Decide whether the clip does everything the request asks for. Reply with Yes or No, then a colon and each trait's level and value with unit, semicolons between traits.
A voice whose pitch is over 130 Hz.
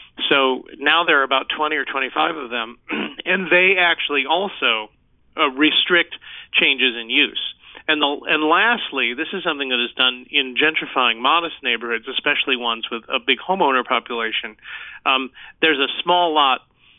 Yes: medium, 140 Hz